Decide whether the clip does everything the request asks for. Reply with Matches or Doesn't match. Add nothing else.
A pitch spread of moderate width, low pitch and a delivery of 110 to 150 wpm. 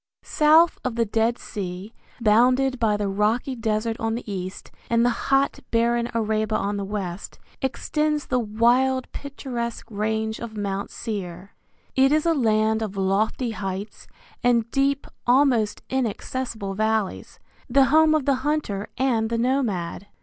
Doesn't match